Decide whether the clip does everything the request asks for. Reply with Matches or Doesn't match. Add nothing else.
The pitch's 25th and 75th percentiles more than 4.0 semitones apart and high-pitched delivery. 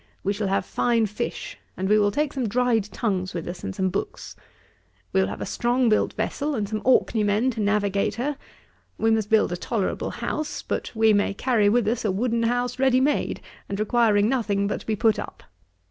Doesn't match